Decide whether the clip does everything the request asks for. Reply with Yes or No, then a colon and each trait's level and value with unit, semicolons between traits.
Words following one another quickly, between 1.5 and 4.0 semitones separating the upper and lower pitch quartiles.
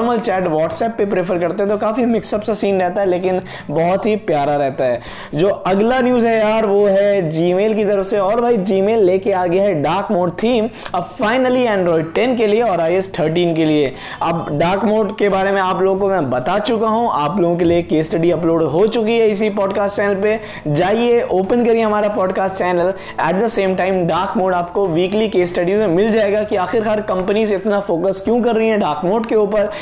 Yes: fast, 220 wpm; average, 3.4 semitones